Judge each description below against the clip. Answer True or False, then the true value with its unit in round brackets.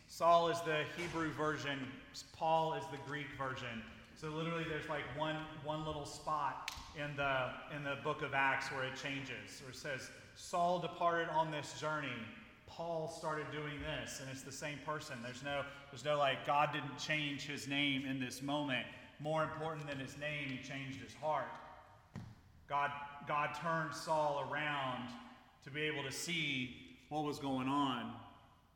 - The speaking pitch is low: False (145 Hz)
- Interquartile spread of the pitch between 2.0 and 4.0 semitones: True (2.5 semitones)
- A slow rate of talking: False (170 wpm)